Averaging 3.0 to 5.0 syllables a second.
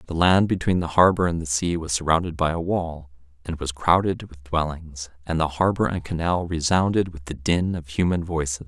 No: 5.2 syllables/s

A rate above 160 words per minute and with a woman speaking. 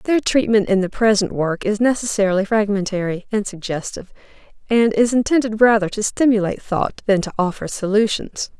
No: average, 155 wpm; female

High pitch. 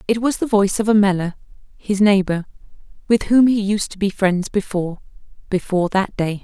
Yes: high, 200 Hz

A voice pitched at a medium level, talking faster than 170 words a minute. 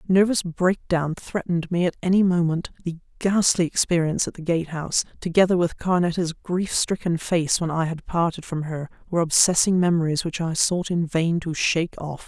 Yes: medium, 170 Hz; average, 180 wpm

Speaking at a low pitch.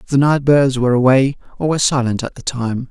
Yes: low, 130 Hz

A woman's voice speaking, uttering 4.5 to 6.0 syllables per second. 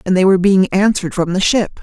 No: female; 6.4 syllables/s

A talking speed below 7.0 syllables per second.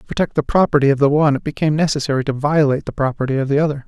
No: 8.1 syllables/s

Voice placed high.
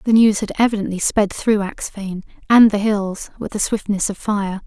Yes: high, 205 Hz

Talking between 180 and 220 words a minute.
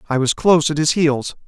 No: fast, 245 wpm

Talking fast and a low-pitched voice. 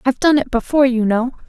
No: fast, 245 wpm; very high, 255 Hz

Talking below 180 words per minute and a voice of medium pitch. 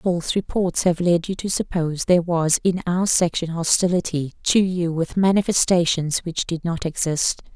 Yes: average, 165 wpm; medium, 175 Hz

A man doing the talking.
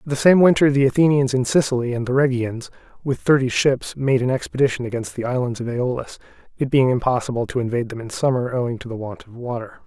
Yes: male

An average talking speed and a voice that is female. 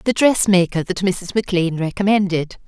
Yes: average, 155 wpm; female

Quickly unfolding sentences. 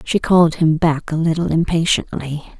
No: average, 160 wpm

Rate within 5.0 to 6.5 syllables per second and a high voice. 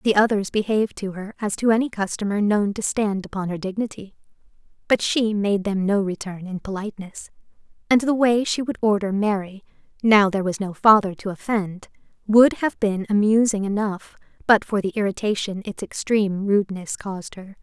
Yes: 5.4 syllables/s; high, 205 Hz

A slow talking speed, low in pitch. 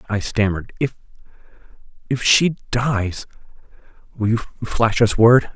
Yes: slow, 120 wpm; low, 115 Hz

